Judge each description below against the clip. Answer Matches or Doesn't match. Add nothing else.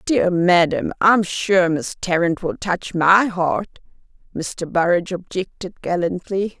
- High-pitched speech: Doesn't match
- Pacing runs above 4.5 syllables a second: Doesn't match